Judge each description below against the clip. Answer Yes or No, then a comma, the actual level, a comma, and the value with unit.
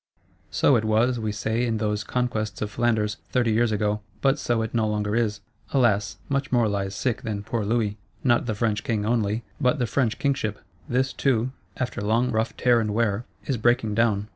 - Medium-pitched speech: No, low, 110 Hz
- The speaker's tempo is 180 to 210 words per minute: Yes, average, 195 wpm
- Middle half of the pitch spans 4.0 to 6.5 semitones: No, narrow, 2.4 semitones